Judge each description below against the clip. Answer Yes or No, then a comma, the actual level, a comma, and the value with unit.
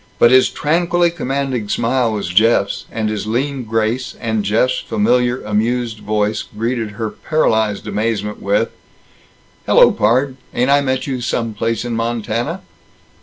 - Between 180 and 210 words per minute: No, average, 140 wpm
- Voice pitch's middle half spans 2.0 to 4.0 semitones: Yes, average, 3.2 semitones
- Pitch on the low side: Yes, low, 115 Hz